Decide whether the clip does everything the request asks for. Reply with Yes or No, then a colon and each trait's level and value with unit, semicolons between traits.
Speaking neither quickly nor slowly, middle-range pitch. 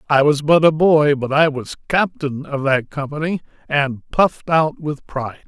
Yes: average, 185 wpm; medium, 150 Hz